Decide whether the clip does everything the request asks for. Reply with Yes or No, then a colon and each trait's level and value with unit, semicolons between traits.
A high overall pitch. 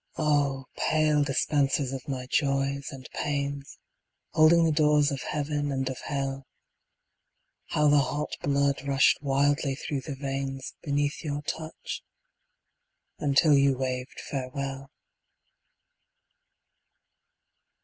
No: medium, 140 Hz